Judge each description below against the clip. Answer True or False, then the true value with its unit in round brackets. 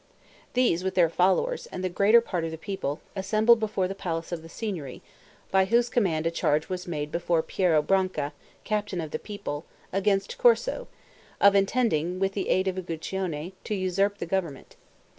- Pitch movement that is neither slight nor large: True (3.6 semitones)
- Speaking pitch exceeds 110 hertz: True (190 Hz)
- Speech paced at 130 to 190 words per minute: True (180 wpm)